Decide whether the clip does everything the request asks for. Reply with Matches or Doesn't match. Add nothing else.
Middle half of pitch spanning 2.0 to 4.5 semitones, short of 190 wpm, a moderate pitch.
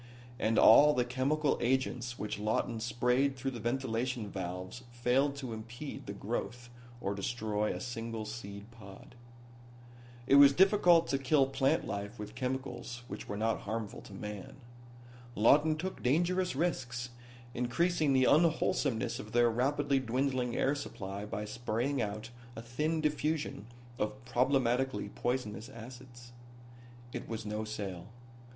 Doesn't match